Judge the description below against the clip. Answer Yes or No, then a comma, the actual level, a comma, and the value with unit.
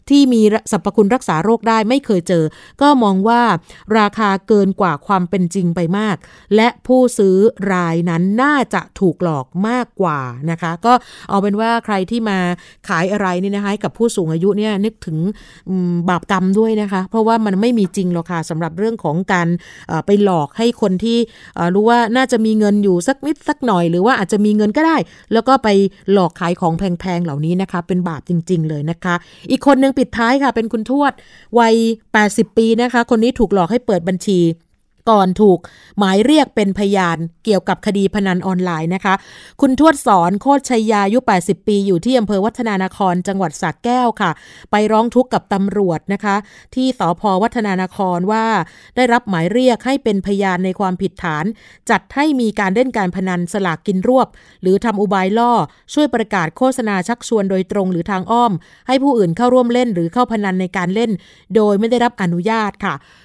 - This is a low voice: No, high, 200 Hz